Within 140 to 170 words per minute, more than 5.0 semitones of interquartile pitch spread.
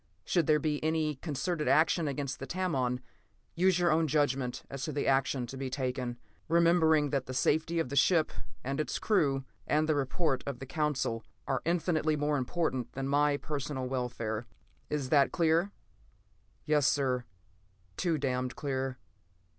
No: average, 160 wpm; average, 3.2 semitones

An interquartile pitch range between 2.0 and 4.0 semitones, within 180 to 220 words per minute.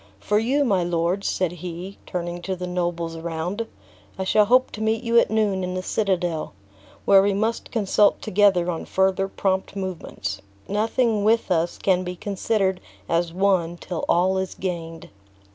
No: average, 2.9 semitones; average, 165 wpm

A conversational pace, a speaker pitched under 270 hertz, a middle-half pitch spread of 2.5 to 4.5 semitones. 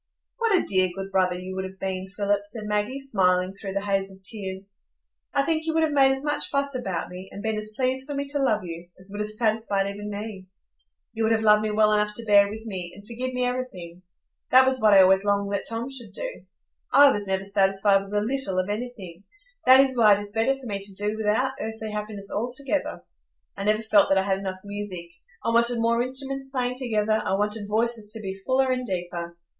No: fast, 230 wpm; high, 210 Hz; average, 4.2 semitones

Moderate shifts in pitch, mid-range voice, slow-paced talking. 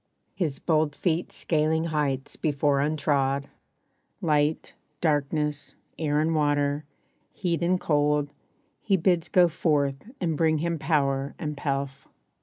No: narrow, 2.2 semitones; medium, 150 Hz; slow, 120 wpm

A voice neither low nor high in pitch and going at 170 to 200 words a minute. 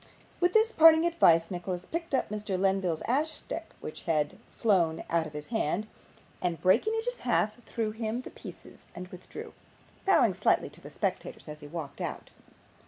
No: high, 205 Hz; average, 175 wpm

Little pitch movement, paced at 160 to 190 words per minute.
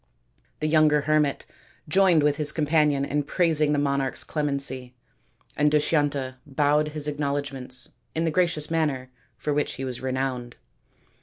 No: narrow, 1.9 semitones; average, 145 wpm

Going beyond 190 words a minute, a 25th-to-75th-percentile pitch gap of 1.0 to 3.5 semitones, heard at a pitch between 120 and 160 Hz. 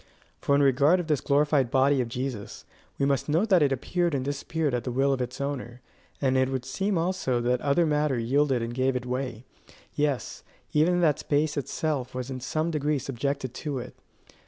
Yes: average, 200 wpm; average, 2.7 semitones; medium, 140 Hz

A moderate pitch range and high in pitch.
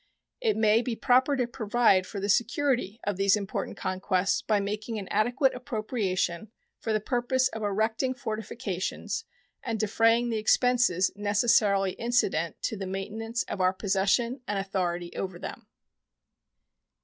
Yes: average, 3.7 semitones; high, 215 Hz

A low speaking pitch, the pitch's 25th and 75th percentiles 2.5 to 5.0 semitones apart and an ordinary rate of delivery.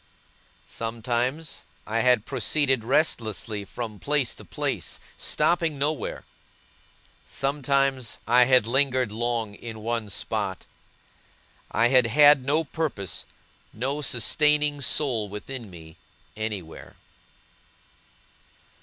No: low, 125 Hz; average, 4.3 semitones; slow, 95 wpm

